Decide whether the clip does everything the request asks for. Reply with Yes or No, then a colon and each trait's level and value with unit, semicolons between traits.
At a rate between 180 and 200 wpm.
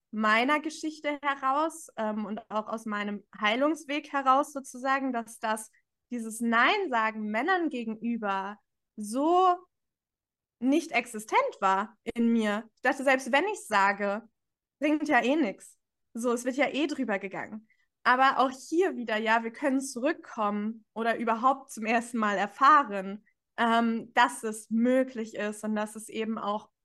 No: average, 145 wpm